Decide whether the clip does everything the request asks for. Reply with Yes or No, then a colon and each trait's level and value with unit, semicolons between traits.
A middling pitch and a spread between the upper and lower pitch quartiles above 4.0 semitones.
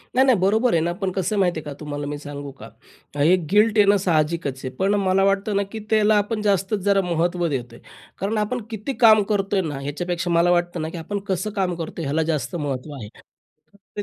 Yes: medium, 180 Hz; average, 4.5 semitones